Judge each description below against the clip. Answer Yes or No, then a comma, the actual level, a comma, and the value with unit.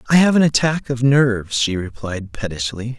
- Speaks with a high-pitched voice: No, low, 120 Hz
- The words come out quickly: No, average, 180 wpm